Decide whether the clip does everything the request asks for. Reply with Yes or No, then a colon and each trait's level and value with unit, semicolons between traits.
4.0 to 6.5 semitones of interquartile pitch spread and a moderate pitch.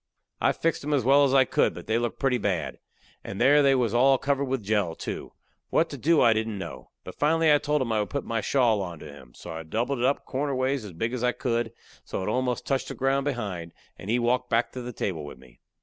No: average, 4.5 semitones; low, 125 Hz